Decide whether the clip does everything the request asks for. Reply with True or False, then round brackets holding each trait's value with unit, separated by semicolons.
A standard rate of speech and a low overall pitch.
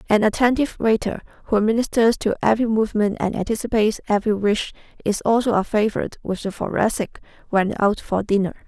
False (160 wpm; 215 Hz)